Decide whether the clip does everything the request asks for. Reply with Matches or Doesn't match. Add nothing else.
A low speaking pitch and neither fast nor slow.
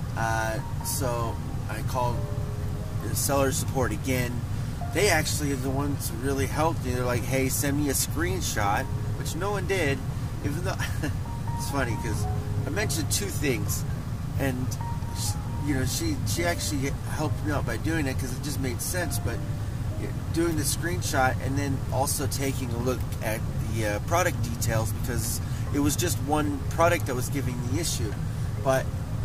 Matches